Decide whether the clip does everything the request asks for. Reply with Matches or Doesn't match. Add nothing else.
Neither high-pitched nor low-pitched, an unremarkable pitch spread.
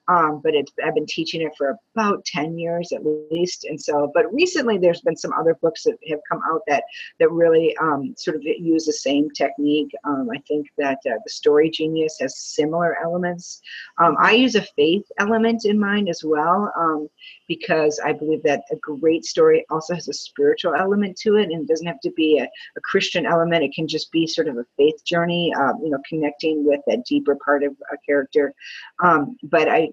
Doesn't match